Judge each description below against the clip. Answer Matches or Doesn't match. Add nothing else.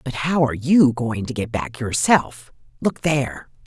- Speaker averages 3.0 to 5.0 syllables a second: Matches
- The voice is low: Matches